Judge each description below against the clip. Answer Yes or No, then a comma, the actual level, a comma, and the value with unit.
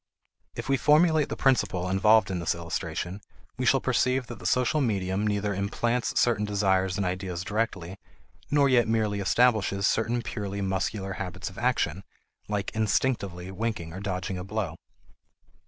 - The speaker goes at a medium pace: Yes, average, 155 wpm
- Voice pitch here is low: Yes, low, 100 Hz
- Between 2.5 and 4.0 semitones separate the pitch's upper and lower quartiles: Yes, average, 3.5 semitones